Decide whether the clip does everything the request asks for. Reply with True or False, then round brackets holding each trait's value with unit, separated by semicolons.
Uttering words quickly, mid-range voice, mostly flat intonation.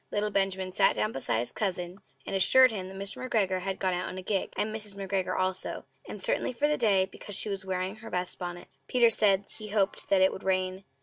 False (235 wpm; 195 Hz; 2.0 semitones)